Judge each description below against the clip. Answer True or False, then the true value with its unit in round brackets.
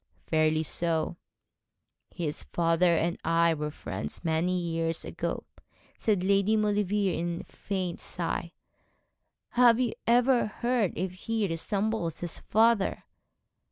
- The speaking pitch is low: False (180 Hz)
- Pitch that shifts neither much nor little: True (4.3 semitones)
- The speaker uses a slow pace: True (120 wpm)